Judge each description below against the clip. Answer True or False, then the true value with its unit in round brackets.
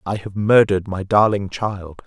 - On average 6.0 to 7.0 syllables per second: False (4.7 syllables/s)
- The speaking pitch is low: True (100 Hz)